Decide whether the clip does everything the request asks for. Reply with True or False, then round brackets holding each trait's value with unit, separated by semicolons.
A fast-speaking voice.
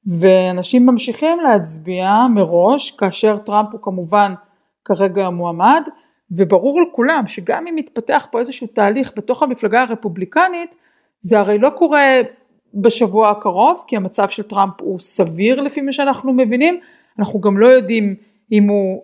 False (135 wpm)